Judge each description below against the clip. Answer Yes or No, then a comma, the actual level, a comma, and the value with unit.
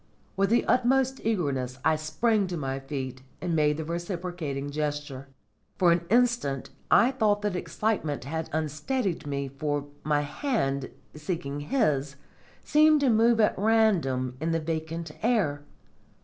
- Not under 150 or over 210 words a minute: No, average, 140 wpm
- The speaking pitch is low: No, medium, 160 Hz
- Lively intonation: Yes, wide, 7.1 semitones